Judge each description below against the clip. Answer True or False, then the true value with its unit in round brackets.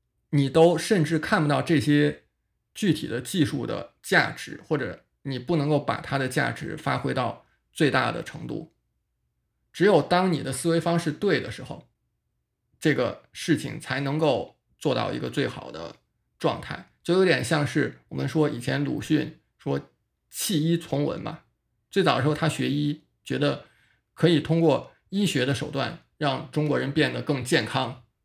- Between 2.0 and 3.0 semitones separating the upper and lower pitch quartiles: True (2.7 semitones)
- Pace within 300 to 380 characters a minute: False (235 characters per minute)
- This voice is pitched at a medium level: True (150 Hz)